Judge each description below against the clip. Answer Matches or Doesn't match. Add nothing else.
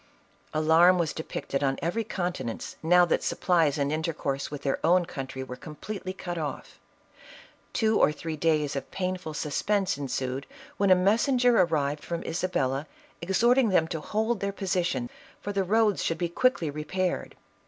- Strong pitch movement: Doesn't match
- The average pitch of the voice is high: Doesn't match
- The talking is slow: Doesn't match